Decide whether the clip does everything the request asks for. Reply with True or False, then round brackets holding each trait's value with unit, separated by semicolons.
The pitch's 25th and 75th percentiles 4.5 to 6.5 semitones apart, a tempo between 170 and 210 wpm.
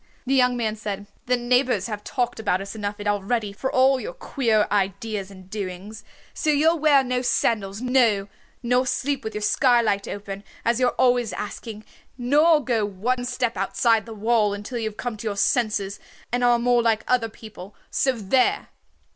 False (3.4 semitones; 180 wpm)